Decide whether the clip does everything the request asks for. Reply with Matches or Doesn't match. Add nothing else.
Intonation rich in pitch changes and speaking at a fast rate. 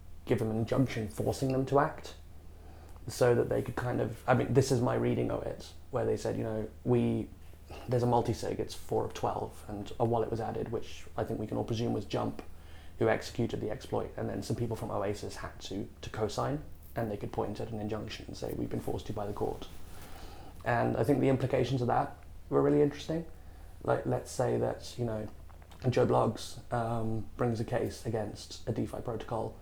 Matches